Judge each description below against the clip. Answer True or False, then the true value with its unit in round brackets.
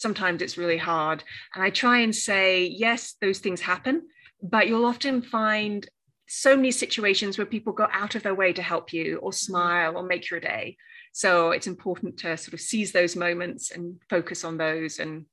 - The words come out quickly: False (195 wpm)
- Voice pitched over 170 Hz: True (190 Hz)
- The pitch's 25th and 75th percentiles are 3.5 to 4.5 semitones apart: True (4.2 semitones)